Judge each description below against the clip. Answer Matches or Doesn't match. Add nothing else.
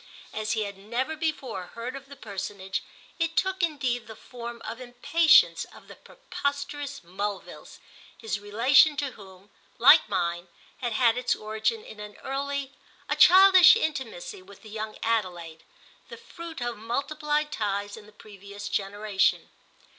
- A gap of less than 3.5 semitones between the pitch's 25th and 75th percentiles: Doesn't match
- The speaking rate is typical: Matches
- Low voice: Doesn't match